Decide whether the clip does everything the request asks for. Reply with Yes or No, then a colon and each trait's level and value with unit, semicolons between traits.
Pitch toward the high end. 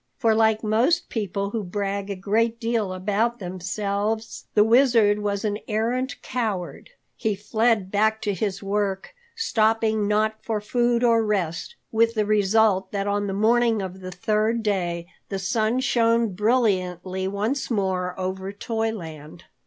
Yes: high, 210 Hz